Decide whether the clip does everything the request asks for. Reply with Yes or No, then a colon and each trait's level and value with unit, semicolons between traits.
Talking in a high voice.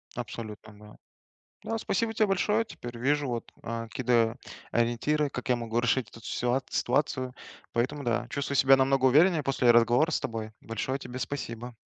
No: low, 125 Hz